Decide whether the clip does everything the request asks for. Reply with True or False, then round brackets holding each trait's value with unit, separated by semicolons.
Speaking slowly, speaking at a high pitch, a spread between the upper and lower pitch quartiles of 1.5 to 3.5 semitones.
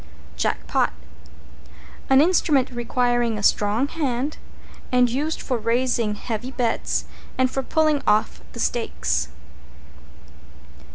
True (110 wpm; 245 Hz; 2.7 semitones)